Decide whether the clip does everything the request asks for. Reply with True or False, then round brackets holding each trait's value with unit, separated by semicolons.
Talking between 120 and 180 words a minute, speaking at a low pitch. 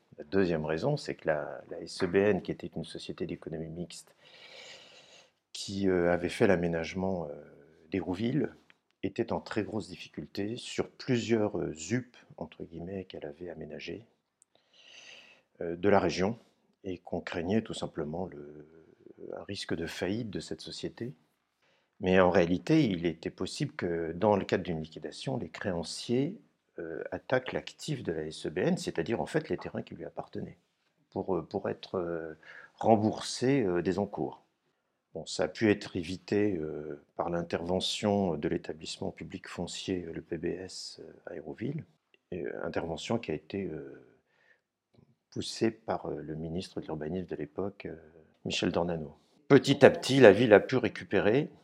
True (145 wpm; 90 Hz)